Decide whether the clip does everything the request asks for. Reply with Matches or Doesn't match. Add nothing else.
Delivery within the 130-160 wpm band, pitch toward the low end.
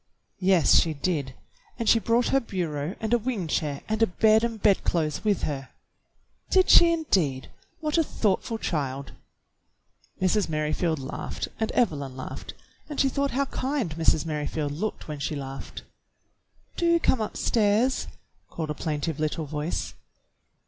Doesn't match